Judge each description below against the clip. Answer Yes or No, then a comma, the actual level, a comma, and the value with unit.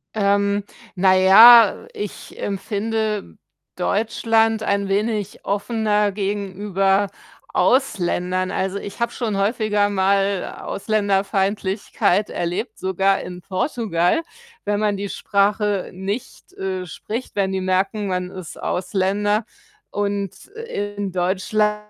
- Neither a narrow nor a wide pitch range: No, narrow, 1.8 semitones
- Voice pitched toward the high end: Yes, high, 200 Hz